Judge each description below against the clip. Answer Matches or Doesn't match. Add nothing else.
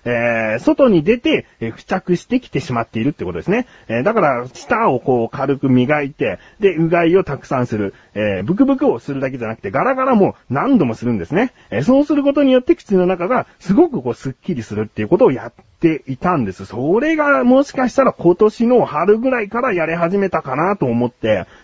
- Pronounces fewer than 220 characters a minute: Doesn't match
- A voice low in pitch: Doesn't match